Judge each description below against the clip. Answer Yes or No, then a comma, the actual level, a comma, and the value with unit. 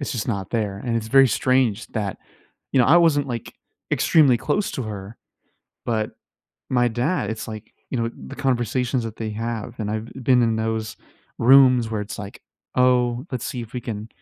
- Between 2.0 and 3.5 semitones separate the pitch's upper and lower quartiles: Yes, average, 2.8 semitones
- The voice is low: Yes, low, 115 Hz